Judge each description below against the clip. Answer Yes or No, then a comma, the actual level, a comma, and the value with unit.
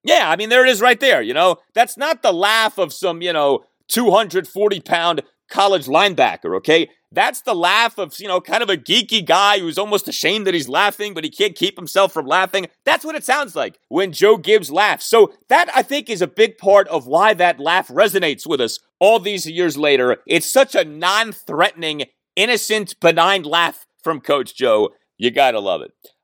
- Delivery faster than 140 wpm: Yes, fast, 205 wpm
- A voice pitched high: Yes, high, 205 Hz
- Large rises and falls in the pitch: Yes, wide, 6.8 semitones